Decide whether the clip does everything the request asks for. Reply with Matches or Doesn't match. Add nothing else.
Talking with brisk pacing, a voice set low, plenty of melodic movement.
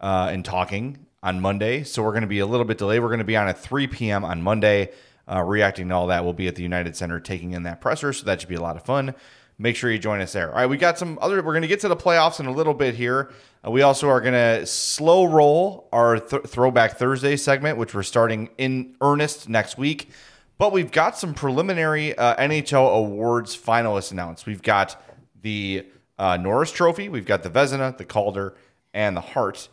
Matches